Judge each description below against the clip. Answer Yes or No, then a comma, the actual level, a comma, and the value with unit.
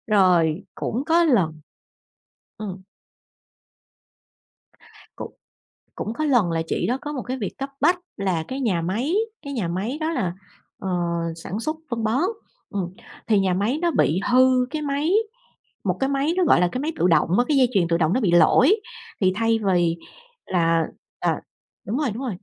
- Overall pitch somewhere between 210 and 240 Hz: Yes, high, 225 Hz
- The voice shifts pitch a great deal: Yes, wide, 7.3 semitones